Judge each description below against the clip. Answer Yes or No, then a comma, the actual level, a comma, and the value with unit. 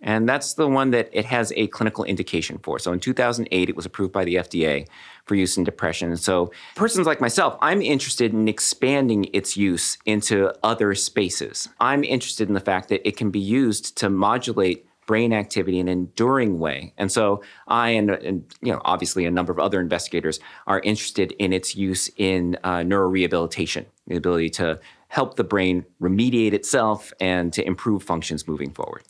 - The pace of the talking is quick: No, average, 190 wpm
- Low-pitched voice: Yes, low, 100 Hz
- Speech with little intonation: No, average, 3.6 semitones